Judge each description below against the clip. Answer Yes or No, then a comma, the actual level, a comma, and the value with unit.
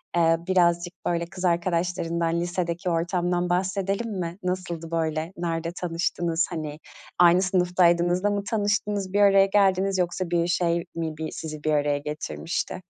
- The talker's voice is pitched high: No, medium, 175 Hz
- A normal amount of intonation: No, narrow, 1.9 semitones